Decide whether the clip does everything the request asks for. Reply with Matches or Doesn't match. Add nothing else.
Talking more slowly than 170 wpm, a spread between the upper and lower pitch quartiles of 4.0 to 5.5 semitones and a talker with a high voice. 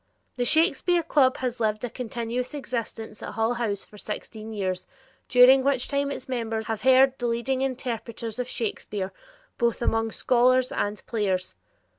Doesn't match